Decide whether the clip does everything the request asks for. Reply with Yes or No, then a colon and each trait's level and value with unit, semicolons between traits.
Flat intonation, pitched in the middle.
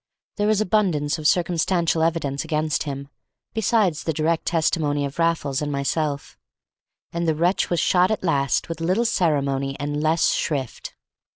No: average, 3.1 semitones; medium, 160 Hz